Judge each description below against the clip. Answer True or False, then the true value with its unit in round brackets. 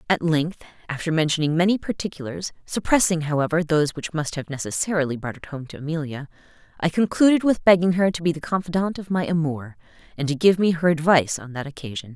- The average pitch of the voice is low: False (160 Hz)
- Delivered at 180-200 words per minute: True (190 wpm)